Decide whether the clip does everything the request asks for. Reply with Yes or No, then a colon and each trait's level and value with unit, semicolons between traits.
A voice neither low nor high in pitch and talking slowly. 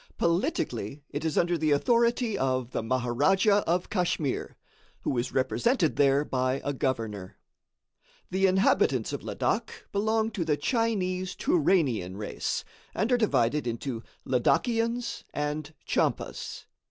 Yes: medium, 155 Hz; slow, 125 wpm